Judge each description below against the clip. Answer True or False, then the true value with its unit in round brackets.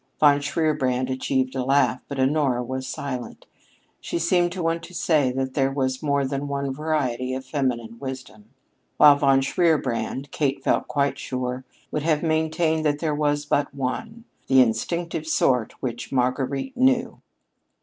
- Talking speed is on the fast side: False (155 wpm)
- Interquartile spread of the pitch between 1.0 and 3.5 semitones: True (3.0 semitones)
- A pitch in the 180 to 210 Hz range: False (140 Hz)